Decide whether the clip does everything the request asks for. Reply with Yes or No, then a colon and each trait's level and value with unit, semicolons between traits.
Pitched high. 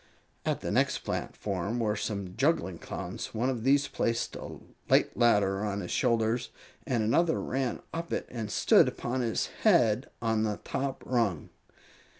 No: low, 115 Hz